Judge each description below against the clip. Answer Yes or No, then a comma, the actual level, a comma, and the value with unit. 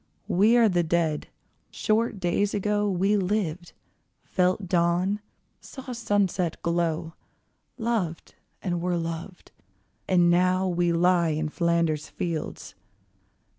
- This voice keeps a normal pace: No, slow, 110 wpm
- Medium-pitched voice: Yes, medium, 180 Hz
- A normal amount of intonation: Yes, average, 3.1 semitones